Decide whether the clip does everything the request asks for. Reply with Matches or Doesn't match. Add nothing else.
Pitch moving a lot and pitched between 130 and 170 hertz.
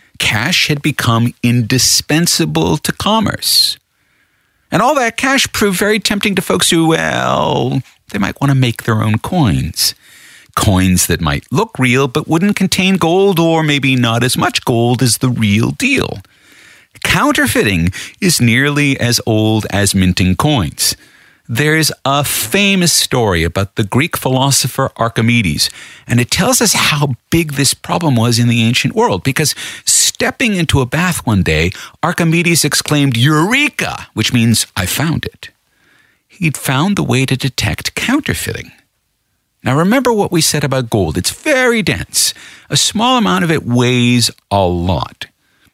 Matches